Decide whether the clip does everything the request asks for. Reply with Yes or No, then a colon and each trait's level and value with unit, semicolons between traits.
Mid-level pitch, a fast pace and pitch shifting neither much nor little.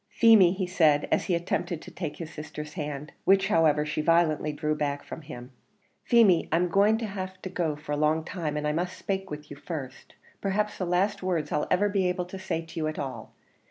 Yes: medium, 165 Hz; fast, 215 wpm; average, 3.9 semitones